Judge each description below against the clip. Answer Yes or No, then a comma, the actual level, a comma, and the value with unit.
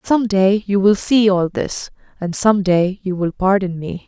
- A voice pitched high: Yes, high, 195 Hz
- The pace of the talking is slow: No, fast, 205 wpm